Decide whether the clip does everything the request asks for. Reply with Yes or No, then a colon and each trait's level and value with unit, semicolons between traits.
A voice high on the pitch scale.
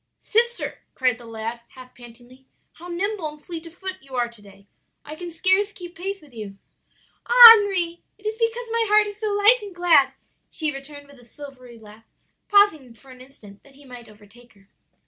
Yes: very high, 295 Hz